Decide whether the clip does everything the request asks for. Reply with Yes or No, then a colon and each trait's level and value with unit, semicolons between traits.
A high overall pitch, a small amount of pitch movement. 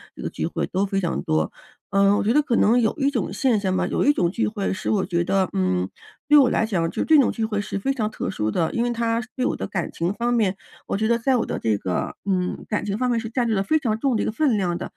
No: high, 215 Hz; average, 4.3 semitones